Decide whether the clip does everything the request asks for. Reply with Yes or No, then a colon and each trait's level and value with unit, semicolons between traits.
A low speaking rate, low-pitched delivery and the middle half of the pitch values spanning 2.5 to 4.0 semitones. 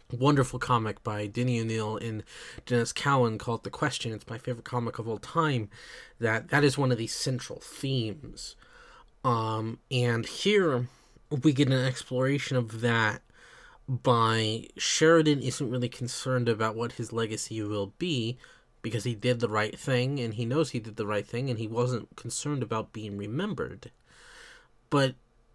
No: average, 160 wpm; low, 120 Hz; average, 2.8 semitones